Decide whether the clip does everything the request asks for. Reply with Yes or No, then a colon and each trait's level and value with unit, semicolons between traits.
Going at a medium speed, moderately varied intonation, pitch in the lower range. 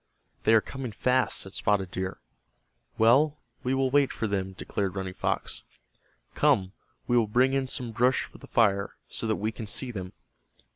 Yes: average, 180 wpm; average, 4.6 semitones; low, 115 Hz